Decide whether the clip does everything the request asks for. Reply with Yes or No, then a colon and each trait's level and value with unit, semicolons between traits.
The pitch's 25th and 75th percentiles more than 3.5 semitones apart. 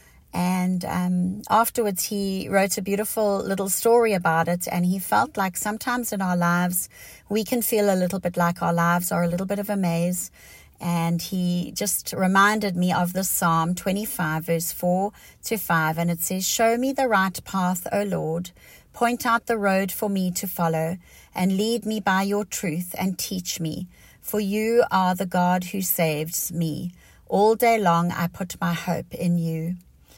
No: average, 2.9 semitones